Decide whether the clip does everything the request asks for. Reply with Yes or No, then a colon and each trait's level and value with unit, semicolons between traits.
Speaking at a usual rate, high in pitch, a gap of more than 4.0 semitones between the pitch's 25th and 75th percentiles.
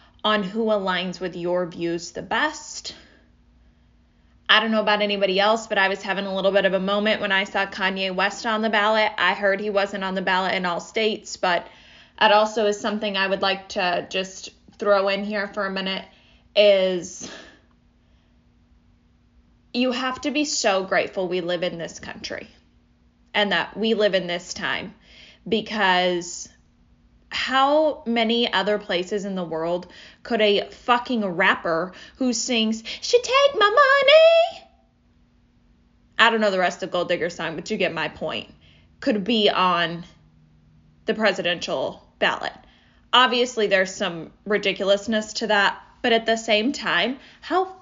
No: average, 160 wpm; high, 195 Hz; average, 3.7 semitones